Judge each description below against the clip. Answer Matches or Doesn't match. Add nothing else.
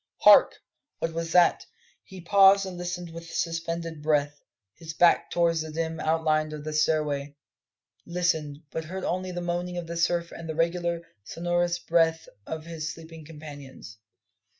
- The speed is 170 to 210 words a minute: Doesn't match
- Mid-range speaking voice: Matches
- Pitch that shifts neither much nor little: Doesn't match